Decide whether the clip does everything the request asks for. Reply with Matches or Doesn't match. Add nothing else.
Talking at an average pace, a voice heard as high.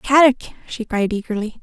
Matches